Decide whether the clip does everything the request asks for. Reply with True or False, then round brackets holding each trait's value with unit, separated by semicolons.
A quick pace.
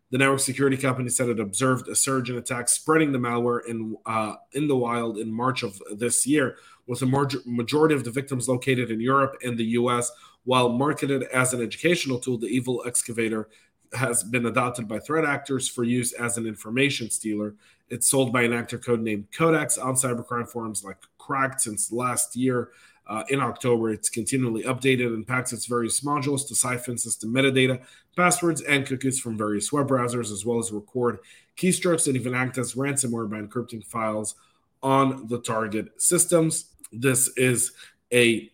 False (180 wpm)